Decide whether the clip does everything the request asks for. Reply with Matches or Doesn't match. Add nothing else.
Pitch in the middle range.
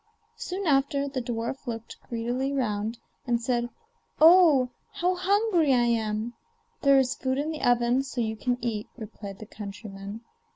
Doesn't match